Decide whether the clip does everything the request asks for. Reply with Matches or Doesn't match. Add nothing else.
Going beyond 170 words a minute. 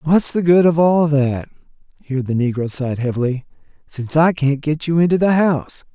Matches